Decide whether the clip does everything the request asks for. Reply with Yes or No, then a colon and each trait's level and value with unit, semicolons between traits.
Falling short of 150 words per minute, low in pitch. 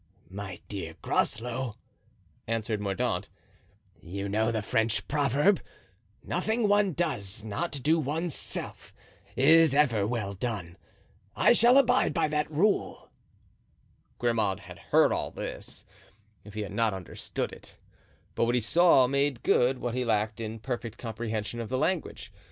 Yes: average, 140 wpm; low, 120 Hz